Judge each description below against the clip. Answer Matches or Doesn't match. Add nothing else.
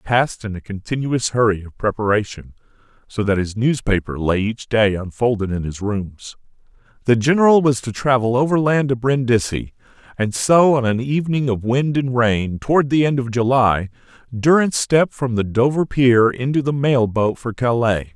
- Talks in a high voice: Doesn't match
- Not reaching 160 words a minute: Doesn't match